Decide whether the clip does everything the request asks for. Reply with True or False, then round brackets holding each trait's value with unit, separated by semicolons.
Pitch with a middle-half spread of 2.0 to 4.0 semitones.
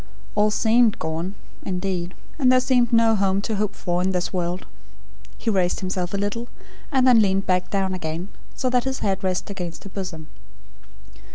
True (3.7 semitones)